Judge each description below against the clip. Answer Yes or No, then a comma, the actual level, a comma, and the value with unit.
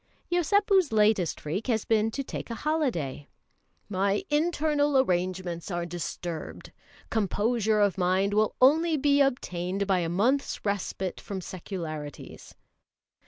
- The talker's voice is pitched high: Yes, high, 205 Hz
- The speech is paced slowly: Yes, slow, 120 wpm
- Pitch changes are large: Yes, wide, 7.2 semitones